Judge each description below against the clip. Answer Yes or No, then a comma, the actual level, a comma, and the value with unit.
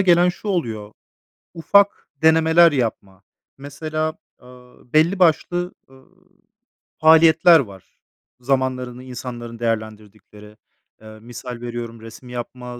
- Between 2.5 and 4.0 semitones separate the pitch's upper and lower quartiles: No, wide, 5.6 semitones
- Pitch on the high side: No, low, 125 Hz